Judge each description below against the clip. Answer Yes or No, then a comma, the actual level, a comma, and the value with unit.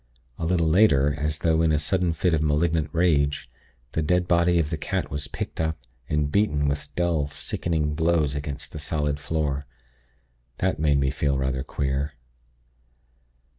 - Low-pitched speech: Yes, very low, 75 Hz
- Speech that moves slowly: No, average, 165 wpm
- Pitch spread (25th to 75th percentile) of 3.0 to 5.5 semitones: No, narrow, 2.4 semitones